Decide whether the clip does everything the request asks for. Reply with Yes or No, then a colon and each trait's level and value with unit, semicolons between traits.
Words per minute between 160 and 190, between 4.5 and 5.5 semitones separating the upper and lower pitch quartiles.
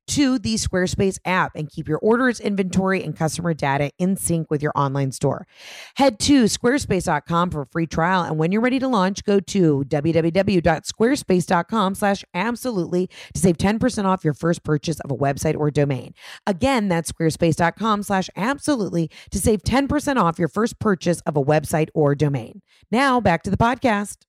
Yes: average, 165 wpm; average, 5.1 semitones